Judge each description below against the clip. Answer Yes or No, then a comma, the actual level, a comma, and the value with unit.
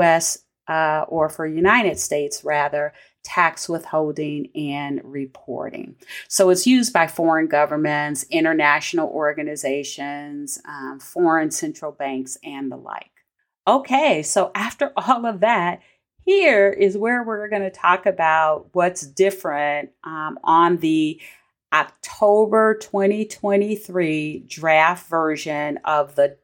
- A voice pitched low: No, medium, 160 Hz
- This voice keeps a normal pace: No, slow, 115 wpm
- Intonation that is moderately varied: Yes, average, 5.0 semitones